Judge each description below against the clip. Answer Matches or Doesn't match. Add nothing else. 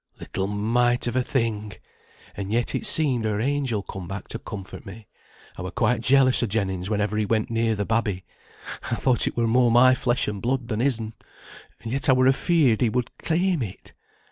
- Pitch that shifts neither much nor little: Matches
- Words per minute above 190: Matches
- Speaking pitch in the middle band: Doesn't match